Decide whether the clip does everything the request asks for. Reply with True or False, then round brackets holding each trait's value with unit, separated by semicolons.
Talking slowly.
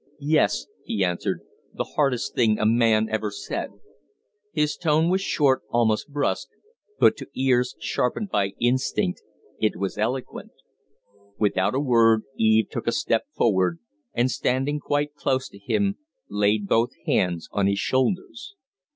False (145 wpm)